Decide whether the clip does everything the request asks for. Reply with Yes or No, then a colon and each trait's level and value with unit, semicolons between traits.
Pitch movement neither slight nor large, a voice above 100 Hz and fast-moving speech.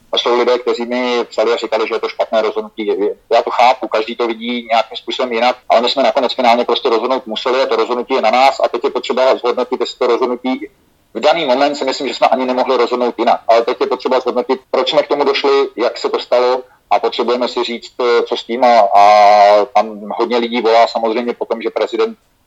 No: narrow, 2.0 semitones; low, 120 Hz; fast, 225 wpm